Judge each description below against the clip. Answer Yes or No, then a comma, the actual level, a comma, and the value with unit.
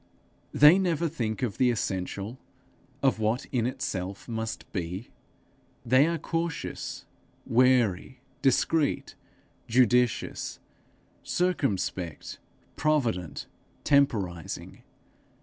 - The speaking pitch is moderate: No, low, 125 Hz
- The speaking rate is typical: No, slow, 80 wpm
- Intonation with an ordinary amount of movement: No, wide, 5.9 semitones